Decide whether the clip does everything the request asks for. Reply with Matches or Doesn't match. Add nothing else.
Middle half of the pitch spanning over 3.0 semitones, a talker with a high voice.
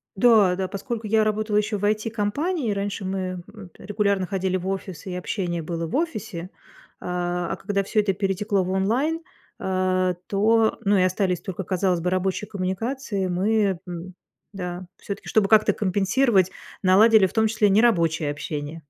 Doesn't match